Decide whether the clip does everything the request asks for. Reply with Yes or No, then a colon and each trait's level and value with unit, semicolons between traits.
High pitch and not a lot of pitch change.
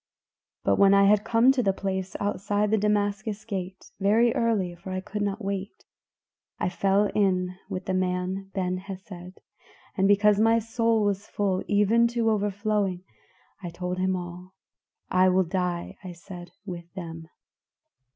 Yes: high, 195 Hz; narrow, 2.2 semitones